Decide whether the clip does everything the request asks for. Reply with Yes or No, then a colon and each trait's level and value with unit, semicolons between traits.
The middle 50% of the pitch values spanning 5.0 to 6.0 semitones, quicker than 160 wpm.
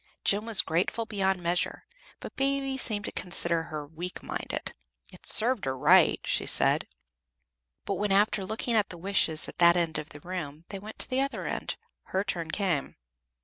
No: average, 4.2 semitones; average, 185 wpm